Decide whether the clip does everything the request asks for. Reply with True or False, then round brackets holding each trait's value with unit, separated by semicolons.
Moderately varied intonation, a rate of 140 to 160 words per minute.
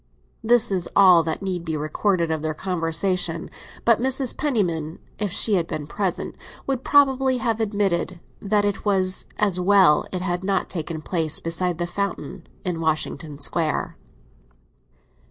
True (3.9 semitones; 150 wpm)